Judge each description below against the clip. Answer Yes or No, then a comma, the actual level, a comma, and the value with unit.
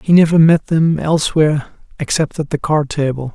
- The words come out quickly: No, average, 180 wpm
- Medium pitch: Yes, medium, 155 Hz